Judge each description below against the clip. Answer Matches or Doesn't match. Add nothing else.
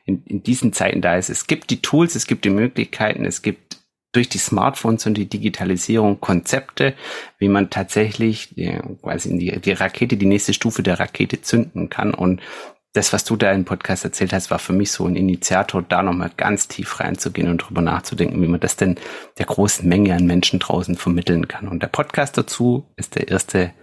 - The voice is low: Matches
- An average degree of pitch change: Matches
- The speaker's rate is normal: Doesn't match